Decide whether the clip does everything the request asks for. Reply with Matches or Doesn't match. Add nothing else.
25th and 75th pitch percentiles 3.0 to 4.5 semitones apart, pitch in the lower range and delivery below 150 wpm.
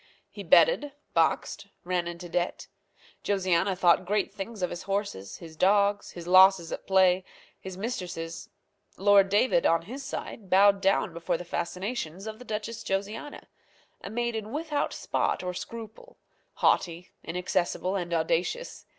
Doesn't match